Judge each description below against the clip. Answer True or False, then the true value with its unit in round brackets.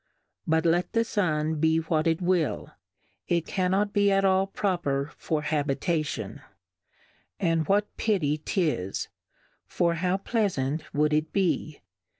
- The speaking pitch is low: False (165 Hz)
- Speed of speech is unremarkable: False (130 wpm)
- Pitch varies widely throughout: False (3.9 semitones)